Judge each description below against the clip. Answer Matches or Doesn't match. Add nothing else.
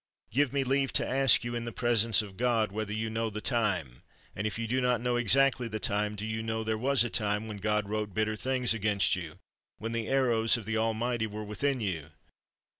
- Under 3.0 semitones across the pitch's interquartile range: Matches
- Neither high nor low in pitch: Doesn't match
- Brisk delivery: Matches